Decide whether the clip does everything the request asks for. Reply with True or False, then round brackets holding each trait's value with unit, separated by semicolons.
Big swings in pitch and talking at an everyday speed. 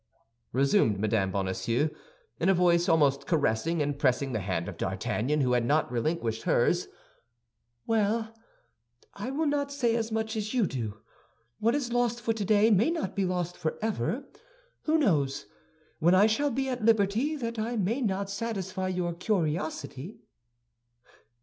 True (8.2 semitones; 150 wpm)